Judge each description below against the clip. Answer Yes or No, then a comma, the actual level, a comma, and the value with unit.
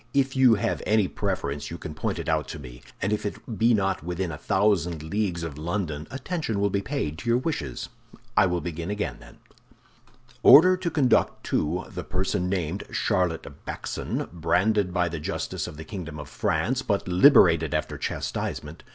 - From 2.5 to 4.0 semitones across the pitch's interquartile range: No, average, 4.9 semitones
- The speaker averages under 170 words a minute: No, average, 175 wpm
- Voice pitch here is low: Yes, very low, 90 Hz